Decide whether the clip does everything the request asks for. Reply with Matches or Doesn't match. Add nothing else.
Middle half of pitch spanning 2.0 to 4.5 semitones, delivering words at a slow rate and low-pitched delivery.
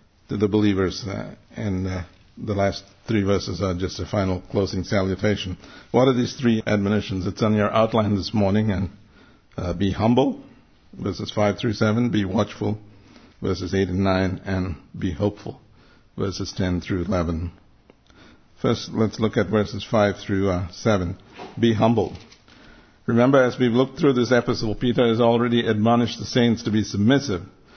Doesn't match